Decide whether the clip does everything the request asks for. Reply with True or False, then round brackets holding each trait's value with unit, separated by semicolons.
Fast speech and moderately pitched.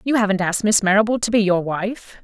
False (240 wpm; 205 Hz)